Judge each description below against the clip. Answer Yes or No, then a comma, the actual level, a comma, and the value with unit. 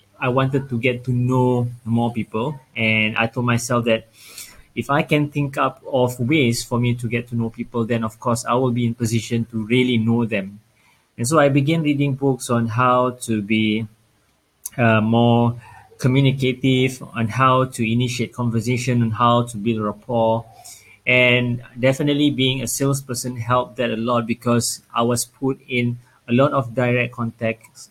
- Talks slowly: No, average, 175 wpm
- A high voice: No, low, 120 Hz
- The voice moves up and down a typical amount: No, narrow, 1.9 semitones